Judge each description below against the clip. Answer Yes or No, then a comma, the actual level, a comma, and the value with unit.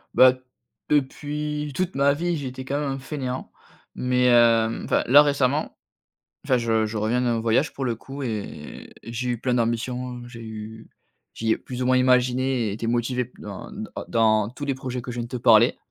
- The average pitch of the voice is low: Yes, low, 125 Hz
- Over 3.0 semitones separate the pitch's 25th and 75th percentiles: No, narrow, 2.6 semitones